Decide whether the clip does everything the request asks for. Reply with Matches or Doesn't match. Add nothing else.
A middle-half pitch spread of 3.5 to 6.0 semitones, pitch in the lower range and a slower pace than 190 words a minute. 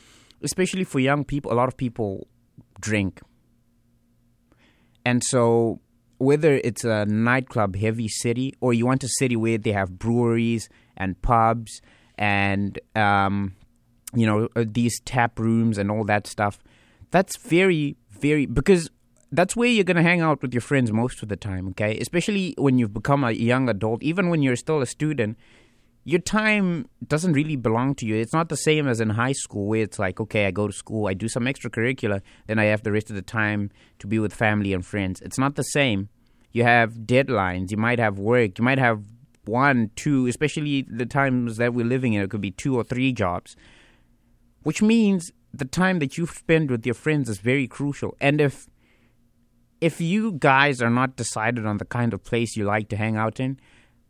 Doesn't match